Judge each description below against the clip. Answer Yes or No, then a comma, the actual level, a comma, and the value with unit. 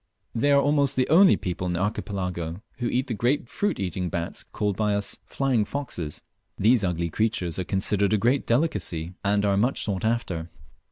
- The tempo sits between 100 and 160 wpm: No, average, 185 wpm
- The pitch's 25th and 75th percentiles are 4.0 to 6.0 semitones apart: Yes, average, 5.3 semitones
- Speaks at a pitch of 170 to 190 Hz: No, low, 105 Hz